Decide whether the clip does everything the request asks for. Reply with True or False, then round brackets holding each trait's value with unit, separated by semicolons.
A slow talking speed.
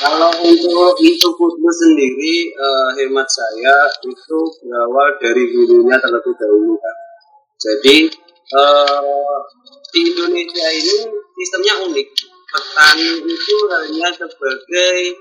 False (100 wpm)